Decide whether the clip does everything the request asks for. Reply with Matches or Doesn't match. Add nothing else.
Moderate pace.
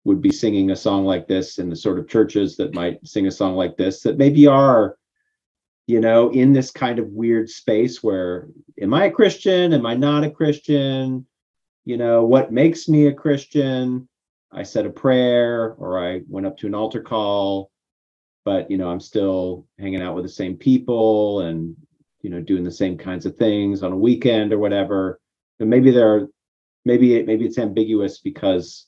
Matches